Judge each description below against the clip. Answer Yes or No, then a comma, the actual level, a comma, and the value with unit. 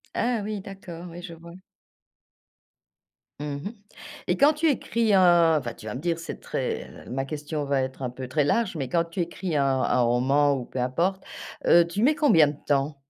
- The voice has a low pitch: No, medium, 165 Hz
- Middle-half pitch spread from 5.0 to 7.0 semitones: Yes, wide, 5.5 semitones